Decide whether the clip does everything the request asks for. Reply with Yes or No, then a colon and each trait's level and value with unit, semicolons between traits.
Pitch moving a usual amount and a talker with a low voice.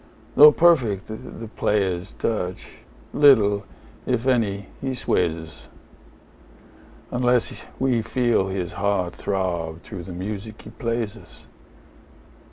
Yes: average, 4.6 semitones; low, 105 Hz